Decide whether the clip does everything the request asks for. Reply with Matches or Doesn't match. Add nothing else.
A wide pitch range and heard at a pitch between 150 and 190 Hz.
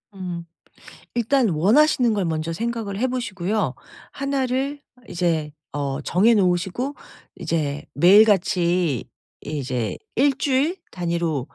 Matches